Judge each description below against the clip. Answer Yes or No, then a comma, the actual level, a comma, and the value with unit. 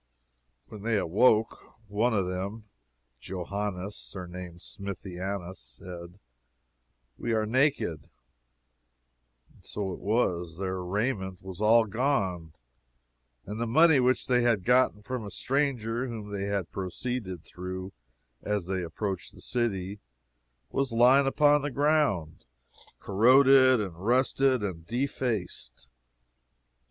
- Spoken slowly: Yes, slow, 115 wpm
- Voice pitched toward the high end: No, low, 105 Hz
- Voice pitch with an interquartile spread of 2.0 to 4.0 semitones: No, average, 5.1 semitones